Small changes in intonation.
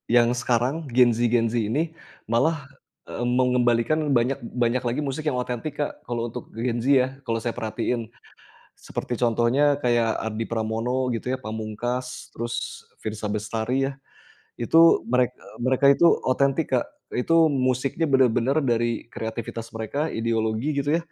Yes: narrow, 2.3 semitones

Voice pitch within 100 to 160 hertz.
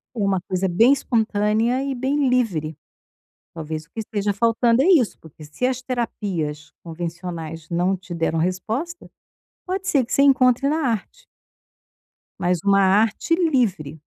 No: high, 210 Hz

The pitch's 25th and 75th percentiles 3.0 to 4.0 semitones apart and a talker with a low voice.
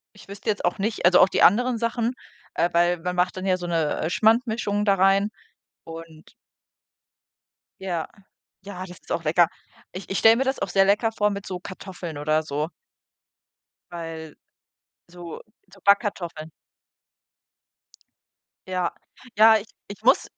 No: average, 3.4 semitones; medium, 185 Hz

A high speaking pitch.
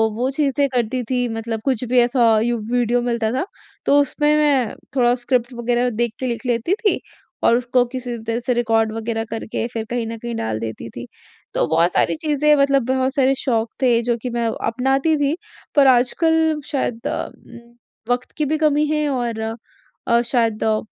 Yes: high, 245 Hz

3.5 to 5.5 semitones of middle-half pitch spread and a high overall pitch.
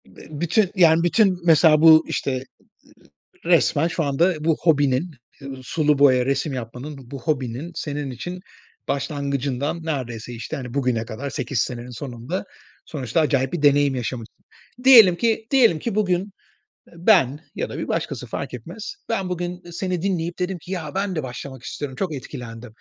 No: average, 5.1 semitones; medium, 150 Hz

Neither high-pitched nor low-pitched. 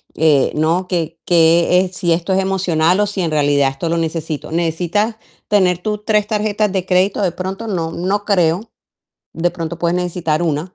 Yes: medium, 175 Hz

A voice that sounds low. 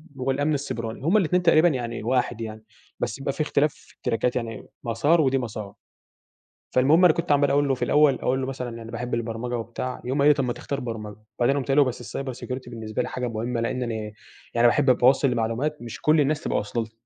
Yes: low, 125 Hz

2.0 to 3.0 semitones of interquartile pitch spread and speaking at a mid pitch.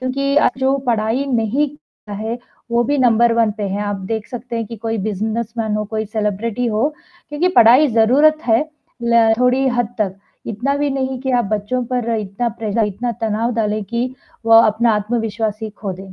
No: average, 2.7 semitones; high, 230 Hz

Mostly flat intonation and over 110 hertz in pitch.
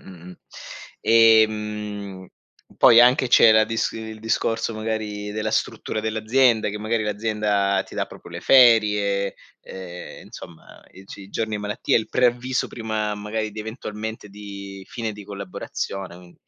No: narrow, 1.8 semitones; low, 105 Hz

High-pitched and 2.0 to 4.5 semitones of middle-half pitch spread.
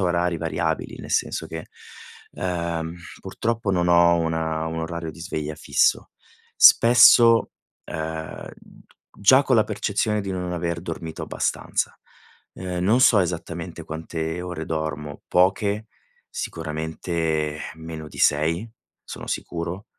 No: very low, 85 Hz; narrow, 2.6 semitones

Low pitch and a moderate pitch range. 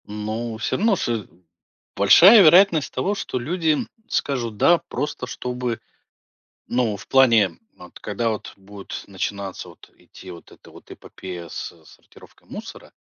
No: low, 115 Hz; wide, 6.5 semitones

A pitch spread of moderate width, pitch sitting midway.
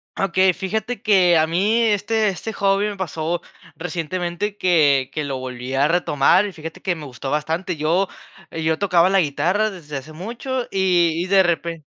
Yes: average, 3.8 semitones; medium, 175 Hz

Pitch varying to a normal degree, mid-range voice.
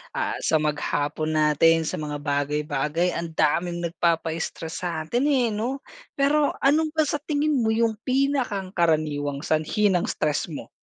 No: wide, 8.1 semitones; medium, 170 Hz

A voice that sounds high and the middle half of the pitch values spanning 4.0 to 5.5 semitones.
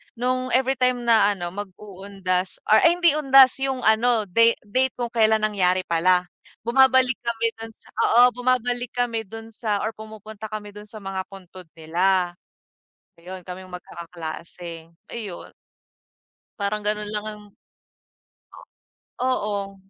Yes: high, 215 Hz; average, 4.3 semitones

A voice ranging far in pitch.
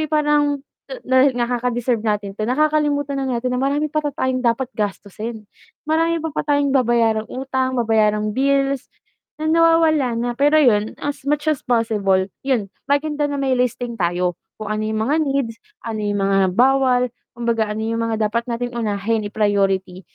No: average, 4.5 semitones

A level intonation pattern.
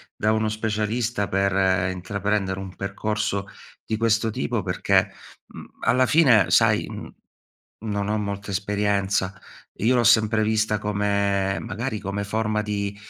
Yes: narrow, 1.6 semitones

